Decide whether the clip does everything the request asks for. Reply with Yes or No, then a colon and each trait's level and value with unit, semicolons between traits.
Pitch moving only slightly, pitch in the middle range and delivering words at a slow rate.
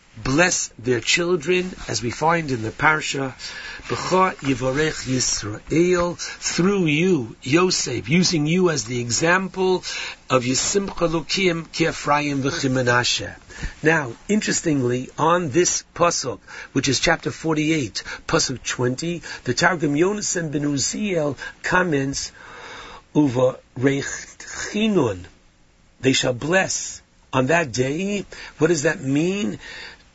No: average, 5.2 semitones; medium, 150 Hz; slow, 105 wpm